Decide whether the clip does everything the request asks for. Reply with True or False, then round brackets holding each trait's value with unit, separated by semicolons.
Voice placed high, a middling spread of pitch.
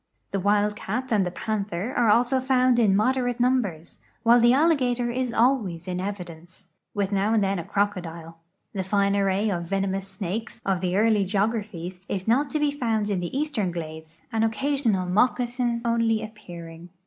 True (210 Hz; 4.2 semitones)